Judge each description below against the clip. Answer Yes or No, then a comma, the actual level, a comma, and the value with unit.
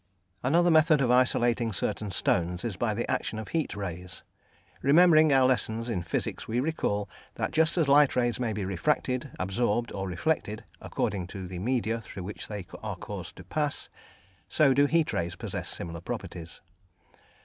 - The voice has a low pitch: Yes, low, 115 Hz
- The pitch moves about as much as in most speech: No, wide, 6.4 semitones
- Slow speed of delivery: No, average, 170 wpm